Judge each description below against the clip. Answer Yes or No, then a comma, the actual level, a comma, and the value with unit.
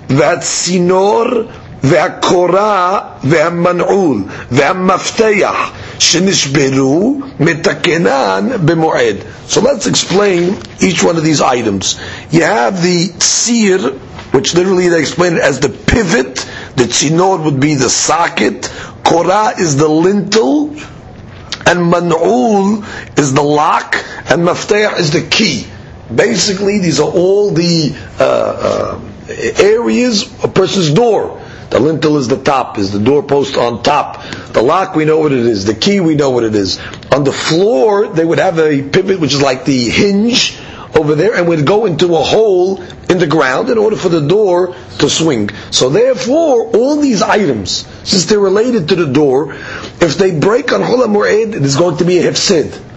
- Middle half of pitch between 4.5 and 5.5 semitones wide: Yes, average, 5.2 semitones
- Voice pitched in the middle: Yes, medium, 175 Hz